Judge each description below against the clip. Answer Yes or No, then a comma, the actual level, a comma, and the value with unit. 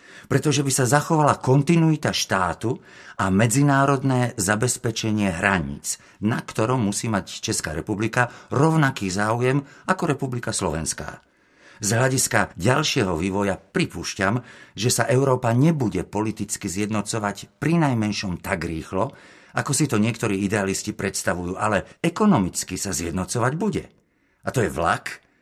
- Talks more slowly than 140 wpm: Yes, average, 120 wpm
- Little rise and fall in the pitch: No, wide, 5.6 semitones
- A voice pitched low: Yes, low, 115 Hz